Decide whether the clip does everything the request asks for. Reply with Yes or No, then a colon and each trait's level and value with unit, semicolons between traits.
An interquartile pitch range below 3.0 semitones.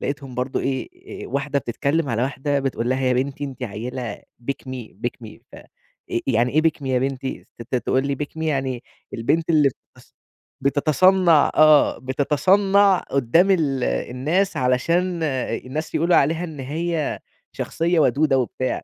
No: average, 3.8 semitones